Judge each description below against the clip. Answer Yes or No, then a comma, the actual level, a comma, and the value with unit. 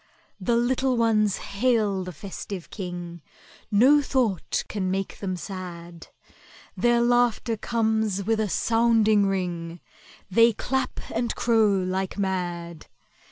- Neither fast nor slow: No, slow, 115 wpm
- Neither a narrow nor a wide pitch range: Yes, average, 4.0 semitones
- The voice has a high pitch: Yes, high, 205 Hz